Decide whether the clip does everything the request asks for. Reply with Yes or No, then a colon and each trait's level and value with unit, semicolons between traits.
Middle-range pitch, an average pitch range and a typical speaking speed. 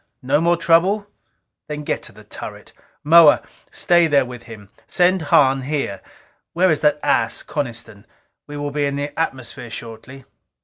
Yes: medium, 145 Hz; average, 4.6 semitones; average, 160 wpm